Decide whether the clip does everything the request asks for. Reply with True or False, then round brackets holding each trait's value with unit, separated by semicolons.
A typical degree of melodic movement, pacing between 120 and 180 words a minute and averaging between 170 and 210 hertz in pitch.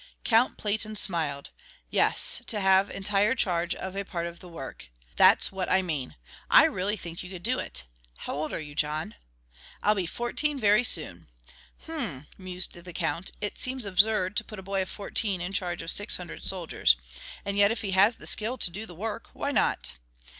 False (3.7 semitones; 195 wpm; 190 Hz)